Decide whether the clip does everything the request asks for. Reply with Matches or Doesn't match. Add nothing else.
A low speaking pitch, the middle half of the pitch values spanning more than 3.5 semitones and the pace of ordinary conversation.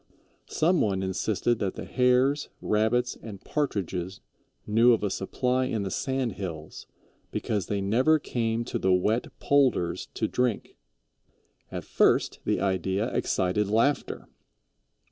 Doesn't match